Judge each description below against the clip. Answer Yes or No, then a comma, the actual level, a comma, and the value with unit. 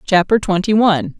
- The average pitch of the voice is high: Yes, high, 195 Hz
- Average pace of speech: Yes, average, 150 wpm